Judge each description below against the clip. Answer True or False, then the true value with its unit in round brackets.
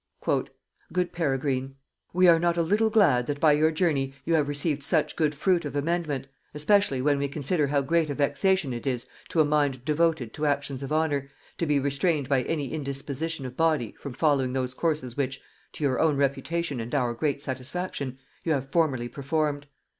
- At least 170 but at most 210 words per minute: True (190 wpm)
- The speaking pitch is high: False (145 Hz)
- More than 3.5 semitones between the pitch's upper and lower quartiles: False (3.1 semitones)